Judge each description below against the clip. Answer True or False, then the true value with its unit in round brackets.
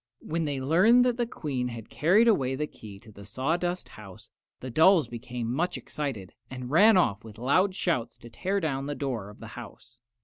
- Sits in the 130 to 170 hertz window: True (135 Hz)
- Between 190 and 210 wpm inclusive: True (200 wpm)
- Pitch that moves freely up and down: True (7.0 semitones)